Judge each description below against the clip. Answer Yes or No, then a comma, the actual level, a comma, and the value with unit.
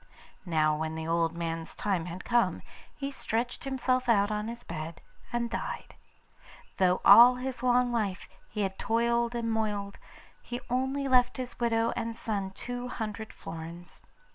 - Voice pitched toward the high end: Yes, high, 225 Hz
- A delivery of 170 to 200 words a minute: No, average, 155 wpm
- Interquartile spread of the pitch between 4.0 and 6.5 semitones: Yes, average, 5.1 semitones